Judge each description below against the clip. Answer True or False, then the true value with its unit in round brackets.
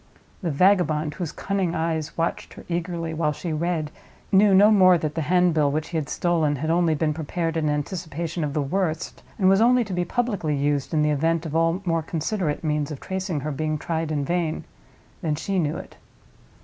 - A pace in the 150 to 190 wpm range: False (200 wpm)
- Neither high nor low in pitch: True (165 Hz)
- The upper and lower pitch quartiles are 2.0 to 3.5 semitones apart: True (2.9 semitones)